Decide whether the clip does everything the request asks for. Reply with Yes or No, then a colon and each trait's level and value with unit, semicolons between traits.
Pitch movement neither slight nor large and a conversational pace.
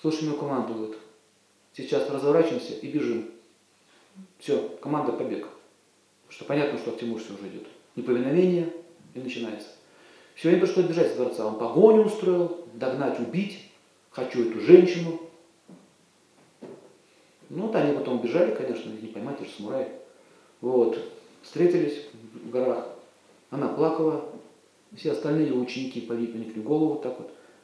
No: wide, 7.0 semitones; average, 135 wpm